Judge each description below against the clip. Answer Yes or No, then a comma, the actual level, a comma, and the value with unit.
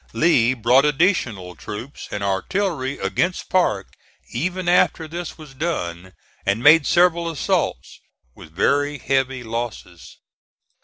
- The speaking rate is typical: No, slow, 115 wpm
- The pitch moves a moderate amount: No, wide, 8.0 semitones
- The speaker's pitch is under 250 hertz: Yes, low, 135 Hz